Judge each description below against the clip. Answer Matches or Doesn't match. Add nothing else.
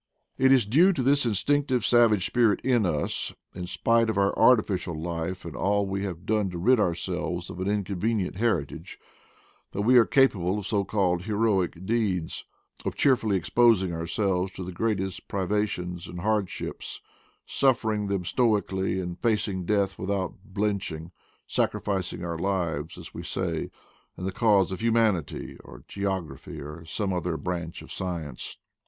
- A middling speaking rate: Matches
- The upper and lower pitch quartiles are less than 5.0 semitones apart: Matches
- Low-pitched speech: Matches